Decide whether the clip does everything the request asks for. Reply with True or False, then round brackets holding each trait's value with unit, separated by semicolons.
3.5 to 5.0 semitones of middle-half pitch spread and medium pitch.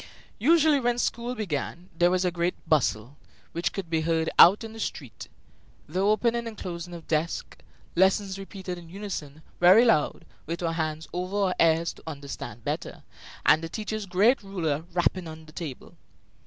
True (4.1 semitones; 175 Hz)